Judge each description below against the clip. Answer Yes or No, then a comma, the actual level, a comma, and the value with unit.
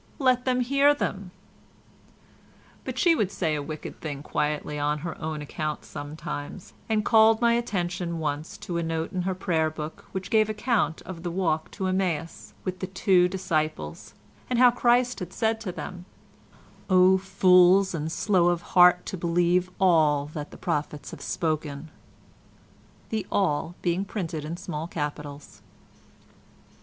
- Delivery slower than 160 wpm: Yes, average, 150 wpm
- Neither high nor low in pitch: Yes, medium, 175 Hz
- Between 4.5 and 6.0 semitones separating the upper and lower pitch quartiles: No, average, 4.0 semitones